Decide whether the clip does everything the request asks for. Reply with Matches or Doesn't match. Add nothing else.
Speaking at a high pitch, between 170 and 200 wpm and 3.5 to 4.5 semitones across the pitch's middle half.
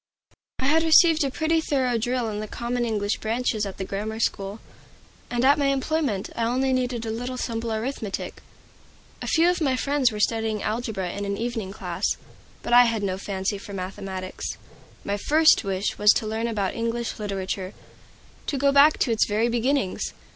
Matches